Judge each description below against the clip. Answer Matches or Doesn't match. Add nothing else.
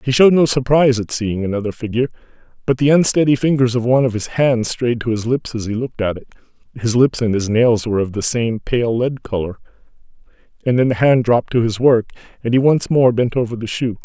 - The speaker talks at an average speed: Doesn't match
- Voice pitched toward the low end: Matches